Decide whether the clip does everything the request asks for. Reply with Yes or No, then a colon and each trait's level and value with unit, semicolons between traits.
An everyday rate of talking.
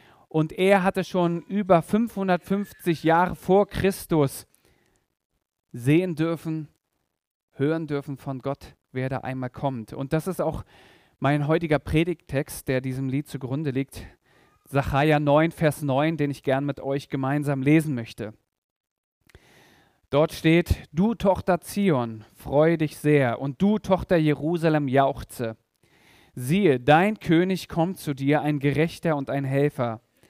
Yes: average, 135 wpm